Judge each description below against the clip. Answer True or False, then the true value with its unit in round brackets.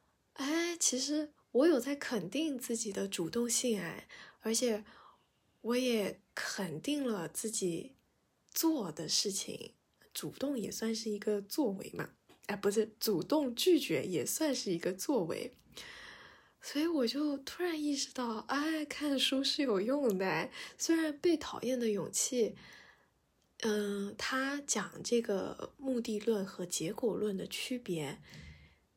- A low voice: False (235 Hz)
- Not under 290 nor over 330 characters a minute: False (190 characters per minute)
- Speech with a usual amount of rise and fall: False (5.7 semitones)